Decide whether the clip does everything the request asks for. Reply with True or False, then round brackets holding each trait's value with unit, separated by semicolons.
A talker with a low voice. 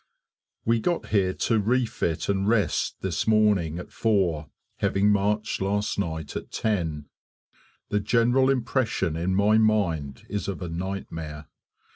True (100 Hz)